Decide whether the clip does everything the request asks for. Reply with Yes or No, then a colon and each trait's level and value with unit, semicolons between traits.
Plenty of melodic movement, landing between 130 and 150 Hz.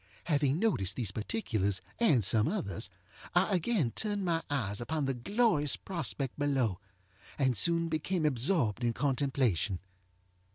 Yes: wide, 6.5 semitones; medium, 140 Hz